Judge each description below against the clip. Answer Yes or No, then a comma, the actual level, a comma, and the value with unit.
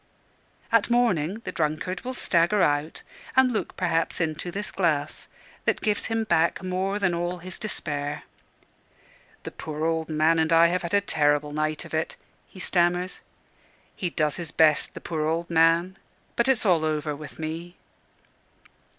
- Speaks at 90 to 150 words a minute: No, average, 160 wpm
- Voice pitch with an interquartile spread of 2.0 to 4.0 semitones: Yes, average, 3.2 semitones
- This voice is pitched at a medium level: Yes, medium, 170 Hz